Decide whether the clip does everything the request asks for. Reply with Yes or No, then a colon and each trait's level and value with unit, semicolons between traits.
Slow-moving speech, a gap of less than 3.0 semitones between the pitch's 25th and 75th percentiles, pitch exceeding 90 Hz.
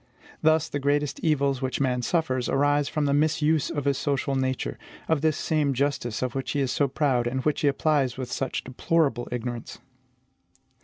No: average, 185 wpm; narrow, 2.5 semitones; medium, 140 Hz